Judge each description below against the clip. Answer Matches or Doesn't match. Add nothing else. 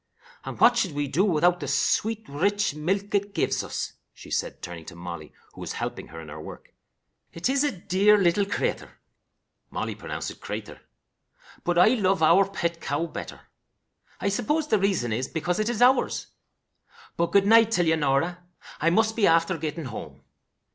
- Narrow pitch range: Doesn't match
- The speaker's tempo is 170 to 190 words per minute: Matches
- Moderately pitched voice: Matches